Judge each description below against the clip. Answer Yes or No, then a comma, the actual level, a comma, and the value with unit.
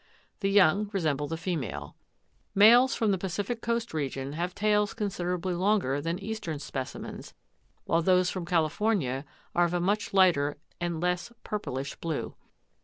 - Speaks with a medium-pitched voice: Yes, medium, 180 Hz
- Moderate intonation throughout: Yes, average, 4.5 semitones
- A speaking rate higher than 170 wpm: No, average, 145 wpm